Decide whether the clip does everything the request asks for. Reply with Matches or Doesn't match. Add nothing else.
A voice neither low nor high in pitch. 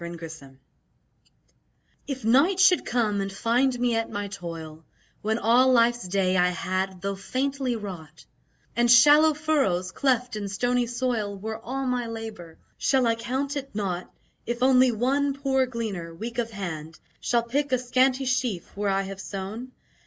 Doesn't match